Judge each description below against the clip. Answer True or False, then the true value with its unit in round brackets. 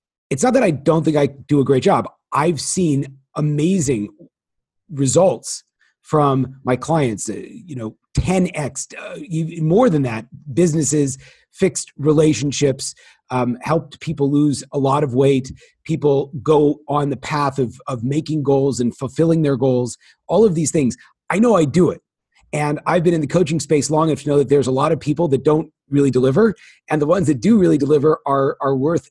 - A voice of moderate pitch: True (145 Hz)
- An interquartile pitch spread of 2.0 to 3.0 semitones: True (2.7 semitones)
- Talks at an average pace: True (185 wpm)